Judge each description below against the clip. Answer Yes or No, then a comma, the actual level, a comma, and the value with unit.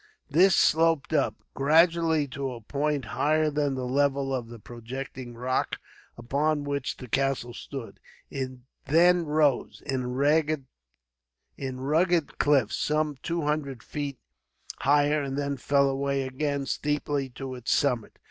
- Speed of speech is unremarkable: No, slow, 130 wpm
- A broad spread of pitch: No, narrow, 2.6 semitones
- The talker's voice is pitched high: No, medium, 140 Hz